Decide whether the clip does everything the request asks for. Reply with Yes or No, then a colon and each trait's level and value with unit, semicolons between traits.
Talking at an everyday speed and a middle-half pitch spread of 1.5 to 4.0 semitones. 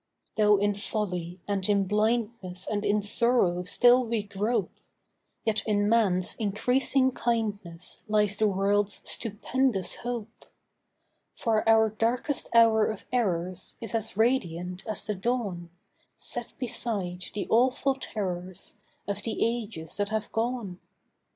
No: slow, 125 wpm; average, 3.2 semitones